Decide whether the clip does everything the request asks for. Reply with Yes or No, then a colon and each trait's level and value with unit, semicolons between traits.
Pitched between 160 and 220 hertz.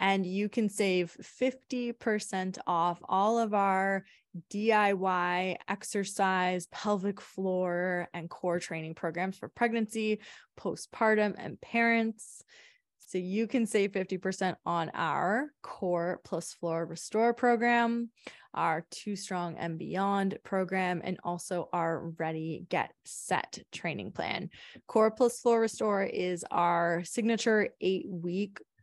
Yes: high, 190 Hz